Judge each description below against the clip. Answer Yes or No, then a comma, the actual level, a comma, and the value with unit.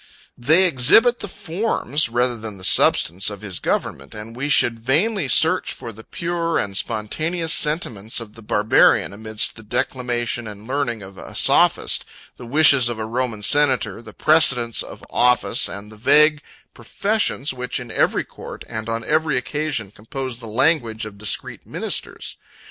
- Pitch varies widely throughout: Yes, wide, 5.7 semitones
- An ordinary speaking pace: Yes, average, 165 wpm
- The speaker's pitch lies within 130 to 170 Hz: No, low, 120 Hz